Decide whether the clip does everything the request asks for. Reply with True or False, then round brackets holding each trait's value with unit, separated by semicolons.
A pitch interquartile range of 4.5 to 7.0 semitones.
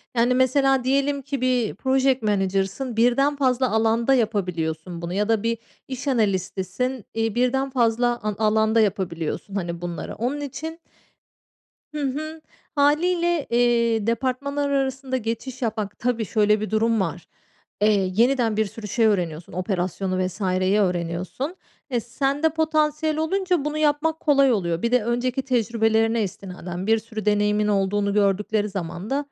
True (4.9 semitones)